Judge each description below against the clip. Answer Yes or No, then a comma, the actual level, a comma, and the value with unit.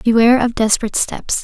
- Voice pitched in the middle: No, high, 230 Hz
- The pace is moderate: Yes, average, 165 wpm